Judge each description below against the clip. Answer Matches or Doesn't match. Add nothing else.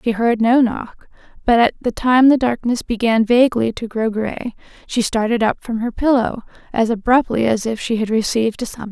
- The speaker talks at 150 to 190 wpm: Doesn't match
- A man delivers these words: Doesn't match